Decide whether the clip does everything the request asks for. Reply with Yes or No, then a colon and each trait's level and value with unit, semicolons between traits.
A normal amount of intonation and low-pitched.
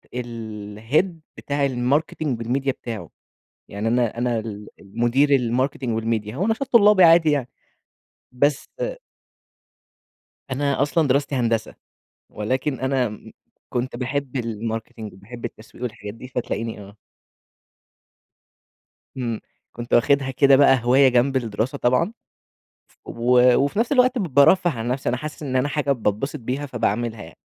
Yes: average, 3.6 semitones; low, 125 Hz